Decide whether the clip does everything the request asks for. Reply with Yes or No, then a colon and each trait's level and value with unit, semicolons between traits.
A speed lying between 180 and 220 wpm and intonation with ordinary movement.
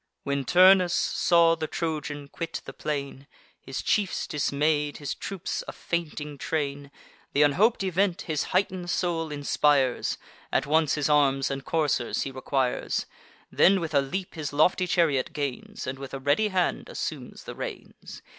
No: average, 155 wpm; average, 3.7 semitones